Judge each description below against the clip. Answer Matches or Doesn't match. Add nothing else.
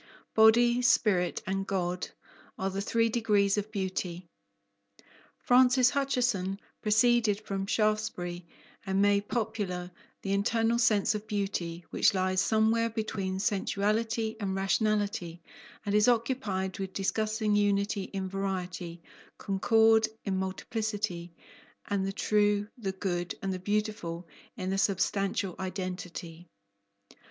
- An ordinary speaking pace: Doesn't match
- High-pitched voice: Matches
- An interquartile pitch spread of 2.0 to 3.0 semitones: Matches